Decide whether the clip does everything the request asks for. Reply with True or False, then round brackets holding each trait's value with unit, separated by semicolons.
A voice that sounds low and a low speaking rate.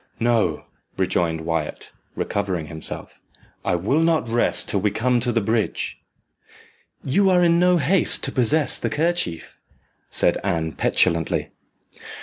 True (115 Hz; 130 wpm)